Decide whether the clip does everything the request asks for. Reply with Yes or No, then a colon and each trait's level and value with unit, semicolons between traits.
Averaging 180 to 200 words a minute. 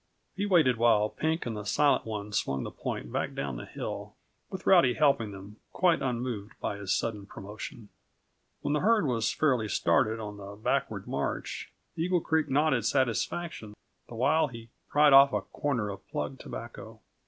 No: average, 170 wpm